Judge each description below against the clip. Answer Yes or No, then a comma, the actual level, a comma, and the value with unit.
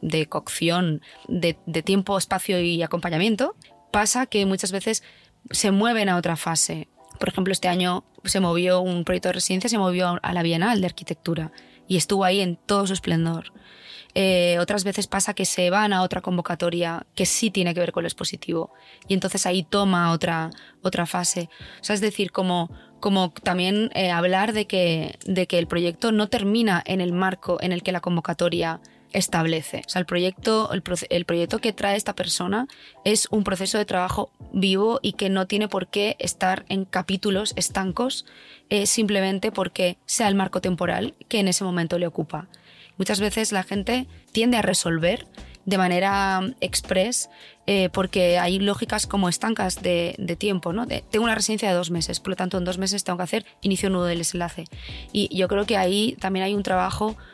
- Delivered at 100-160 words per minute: No, fast, 190 wpm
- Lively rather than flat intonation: No, narrow, 2.6 semitones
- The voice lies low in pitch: No, high, 190 Hz